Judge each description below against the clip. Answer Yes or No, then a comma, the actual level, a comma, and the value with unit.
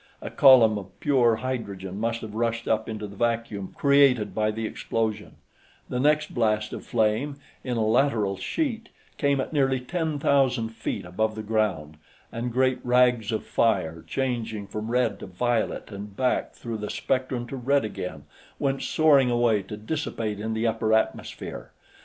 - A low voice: Yes, low, 115 Hz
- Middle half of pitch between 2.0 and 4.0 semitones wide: Yes, average, 3.3 semitones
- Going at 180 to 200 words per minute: No, average, 165 wpm